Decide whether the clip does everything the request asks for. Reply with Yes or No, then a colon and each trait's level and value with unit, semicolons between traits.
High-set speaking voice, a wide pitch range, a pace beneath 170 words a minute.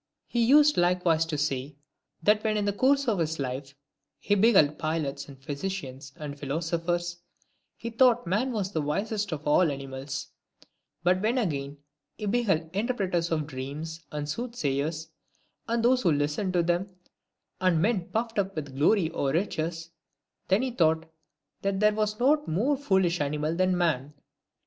No: medium, 175 Hz; wide, 5.9 semitones; average, 160 wpm